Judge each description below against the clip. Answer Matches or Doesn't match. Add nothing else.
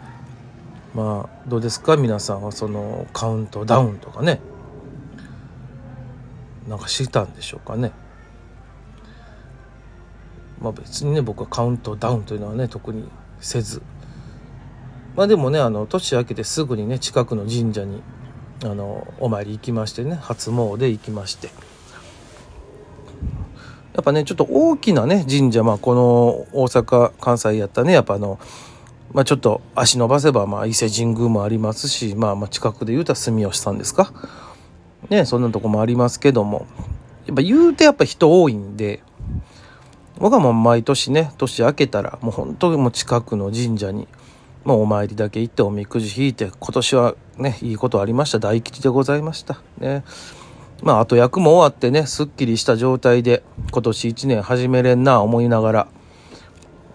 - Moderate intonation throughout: Matches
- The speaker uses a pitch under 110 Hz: Doesn't match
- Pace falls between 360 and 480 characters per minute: Doesn't match